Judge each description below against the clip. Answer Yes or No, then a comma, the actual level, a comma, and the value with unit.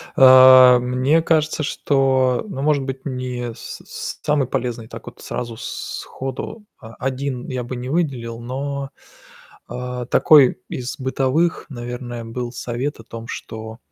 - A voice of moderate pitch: No, low, 130 Hz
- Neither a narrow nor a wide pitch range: No, narrow, 2.0 semitones